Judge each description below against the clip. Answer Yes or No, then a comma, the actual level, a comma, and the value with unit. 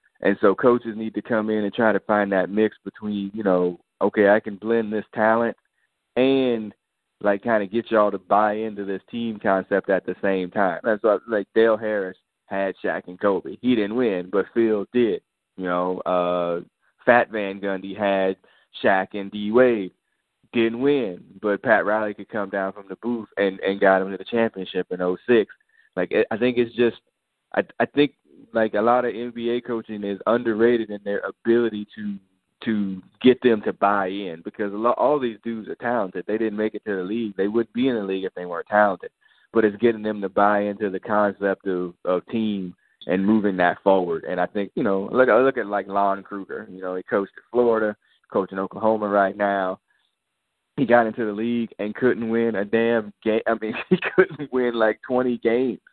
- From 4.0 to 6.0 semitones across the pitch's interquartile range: No, average, 2.9 semitones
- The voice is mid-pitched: No, low, 105 Hz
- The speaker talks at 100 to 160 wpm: No, fast, 205 wpm